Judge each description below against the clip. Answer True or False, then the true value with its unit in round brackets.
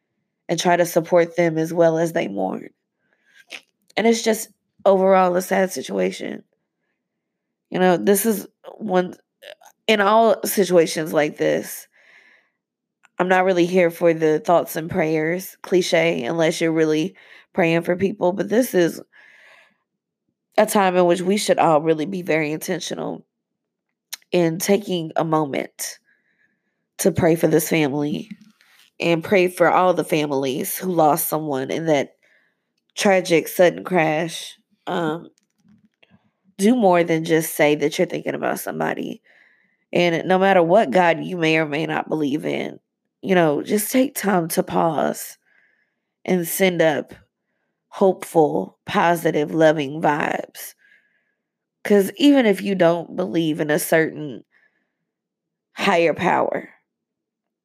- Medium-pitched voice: True (175 Hz)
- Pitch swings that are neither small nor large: True (3.3 semitones)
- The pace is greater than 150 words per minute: False (135 wpm)